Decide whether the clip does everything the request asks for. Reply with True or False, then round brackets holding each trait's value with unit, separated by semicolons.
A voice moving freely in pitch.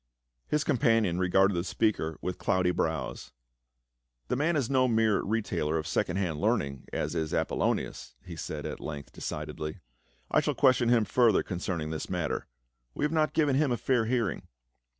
True (7.2 semitones)